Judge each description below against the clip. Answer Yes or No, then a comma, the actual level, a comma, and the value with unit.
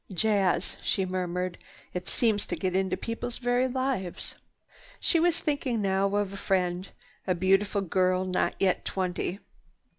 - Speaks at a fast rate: No, average, 145 wpm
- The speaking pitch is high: Yes, high, 195 Hz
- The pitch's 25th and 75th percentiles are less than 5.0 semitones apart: Yes, average, 3.2 semitones